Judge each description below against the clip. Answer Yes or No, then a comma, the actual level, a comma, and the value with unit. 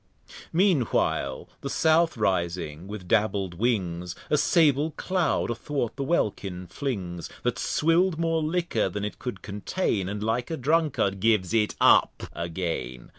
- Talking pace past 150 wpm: No, average, 145 wpm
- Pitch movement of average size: No, wide, 8.9 semitones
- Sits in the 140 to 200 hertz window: No, low, 110 Hz